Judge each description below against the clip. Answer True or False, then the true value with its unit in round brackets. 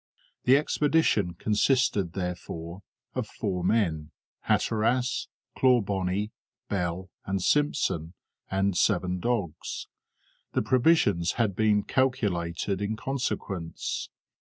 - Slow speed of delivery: True (90 wpm)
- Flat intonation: False (5.1 semitones)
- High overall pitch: False (100 Hz)